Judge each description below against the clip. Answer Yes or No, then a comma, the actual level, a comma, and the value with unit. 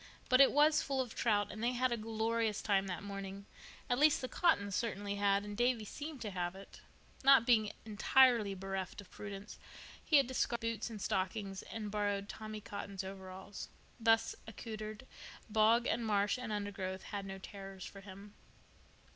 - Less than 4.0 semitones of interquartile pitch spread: Yes, average, 2.9 semitones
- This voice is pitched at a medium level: No, high, 210 Hz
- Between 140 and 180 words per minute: Yes, average, 170 wpm